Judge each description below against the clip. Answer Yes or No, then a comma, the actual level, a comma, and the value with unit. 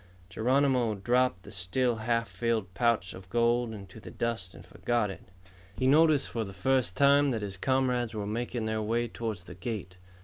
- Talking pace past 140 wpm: Yes, average, 180 wpm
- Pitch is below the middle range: Yes, low, 115 Hz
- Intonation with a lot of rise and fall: No, average, 3.5 semitones